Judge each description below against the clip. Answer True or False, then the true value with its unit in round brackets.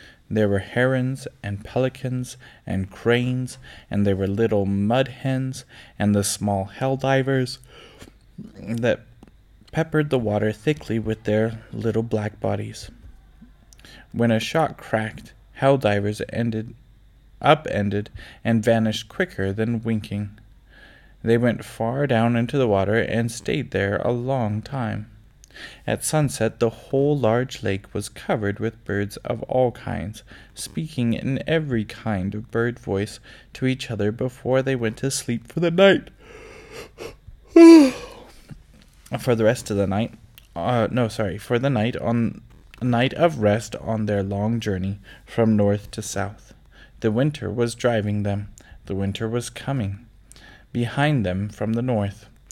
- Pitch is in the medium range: False (115 Hz)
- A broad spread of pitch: False (3.6 semitones)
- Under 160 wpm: True (140 wpm)